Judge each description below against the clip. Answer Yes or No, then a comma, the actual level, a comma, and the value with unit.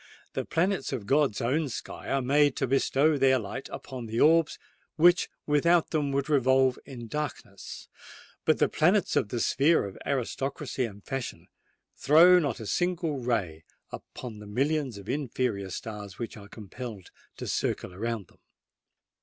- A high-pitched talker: No, low, 130 Hz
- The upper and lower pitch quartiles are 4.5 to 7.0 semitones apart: Yes, average, 4.8 semitones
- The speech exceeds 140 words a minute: Yes, average, 155 wpm